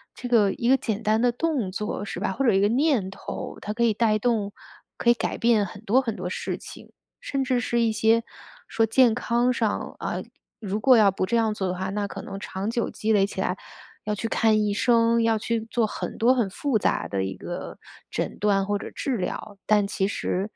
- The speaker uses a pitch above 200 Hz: Yes, high, 220 Hz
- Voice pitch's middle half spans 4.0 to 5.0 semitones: No, average, 2.8 semitones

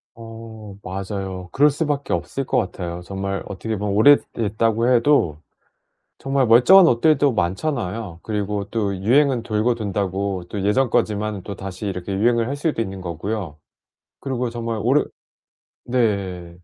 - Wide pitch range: No, average, 4.0 semitones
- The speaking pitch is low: Yes, low, 110 Hz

